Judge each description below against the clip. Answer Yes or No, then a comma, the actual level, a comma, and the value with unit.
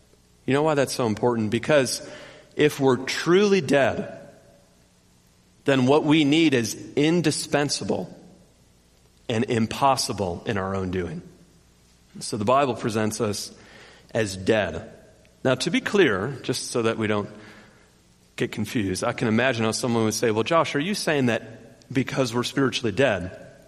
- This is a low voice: Yes, low, 115 Hz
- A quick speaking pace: No, average, 145 wpm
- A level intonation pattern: No, average, 5.2 semitones